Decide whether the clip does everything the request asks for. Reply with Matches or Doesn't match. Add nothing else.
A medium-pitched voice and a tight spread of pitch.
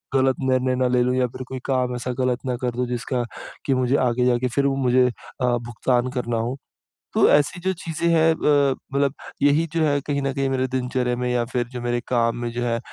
Doesn't match